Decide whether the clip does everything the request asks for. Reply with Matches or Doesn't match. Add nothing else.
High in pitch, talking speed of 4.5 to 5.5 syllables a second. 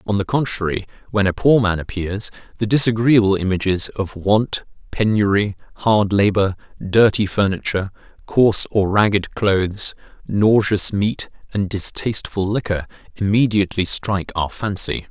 Doesn't match